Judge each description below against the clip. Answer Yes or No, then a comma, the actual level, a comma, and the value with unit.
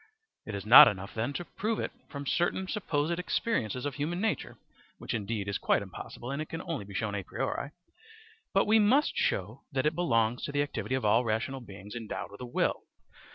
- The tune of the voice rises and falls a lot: Yes, wide, 7.2 semitones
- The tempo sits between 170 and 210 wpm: Yes, fast, 205 wpm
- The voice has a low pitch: Yes, low, 130 Hz